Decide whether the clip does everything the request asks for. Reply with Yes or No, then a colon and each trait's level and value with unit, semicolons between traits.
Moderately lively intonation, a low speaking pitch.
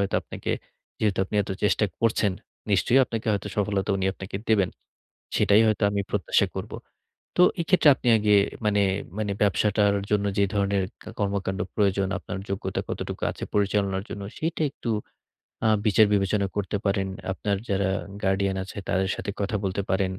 No: narrow, 1.3 semitones; low, 100 Hz